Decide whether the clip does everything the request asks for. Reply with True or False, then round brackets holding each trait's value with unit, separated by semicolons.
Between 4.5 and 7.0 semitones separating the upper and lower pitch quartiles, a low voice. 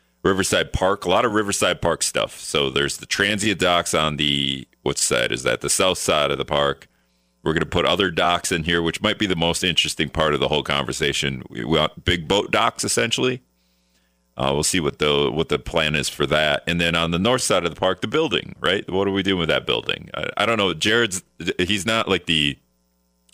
True (5.6 semitones; 85 Hz)